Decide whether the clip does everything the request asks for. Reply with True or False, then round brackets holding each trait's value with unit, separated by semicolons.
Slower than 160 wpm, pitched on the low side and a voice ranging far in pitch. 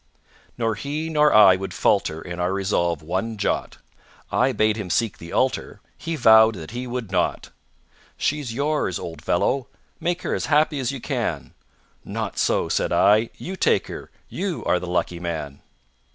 False (170 wpm; 110 Hz; 7.7 semitones)